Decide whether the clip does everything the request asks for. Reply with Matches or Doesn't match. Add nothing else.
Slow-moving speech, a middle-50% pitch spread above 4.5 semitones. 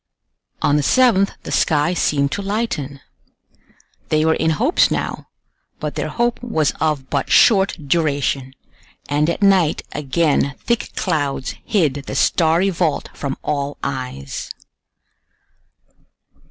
Matches